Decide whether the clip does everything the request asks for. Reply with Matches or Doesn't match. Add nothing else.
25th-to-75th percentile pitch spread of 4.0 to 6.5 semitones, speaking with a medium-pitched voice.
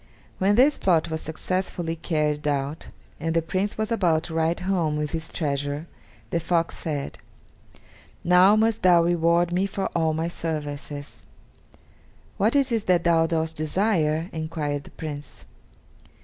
Doesn't match